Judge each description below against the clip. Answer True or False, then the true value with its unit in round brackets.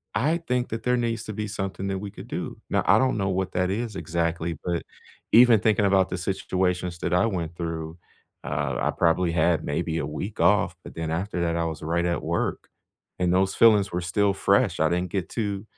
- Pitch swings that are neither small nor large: True (3.4 semitones)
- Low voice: True (90 Hz)